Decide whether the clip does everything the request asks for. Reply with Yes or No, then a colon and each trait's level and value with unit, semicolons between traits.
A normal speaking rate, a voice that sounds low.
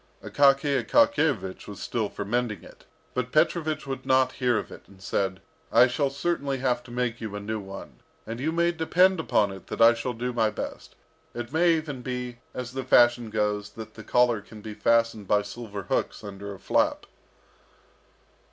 Yes: average, 190 wpm; low, 120 Hz